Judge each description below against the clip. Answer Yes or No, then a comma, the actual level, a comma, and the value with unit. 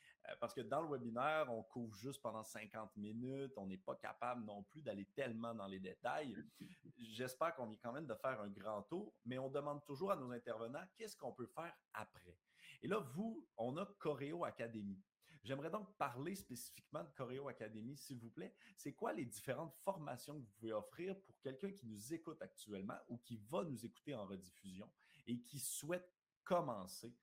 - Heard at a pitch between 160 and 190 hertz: No, low, 125 Hz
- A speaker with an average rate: Yes, average, 195 wpm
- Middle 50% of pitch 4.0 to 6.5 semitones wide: Yes, average, 5.1 semitones